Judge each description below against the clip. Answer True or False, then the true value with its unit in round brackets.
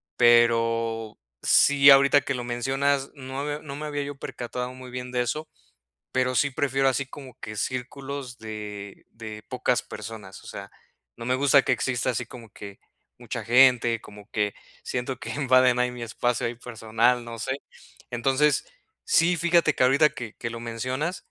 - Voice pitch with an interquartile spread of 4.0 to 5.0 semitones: False (3.0 semitones)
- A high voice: False (125 Hz)